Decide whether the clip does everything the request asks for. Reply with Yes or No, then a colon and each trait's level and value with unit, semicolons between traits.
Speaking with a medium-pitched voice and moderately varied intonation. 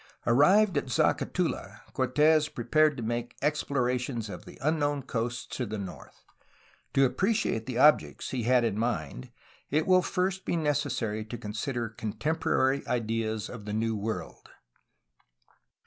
No: low, 125 Hz; average, 4.9 semitones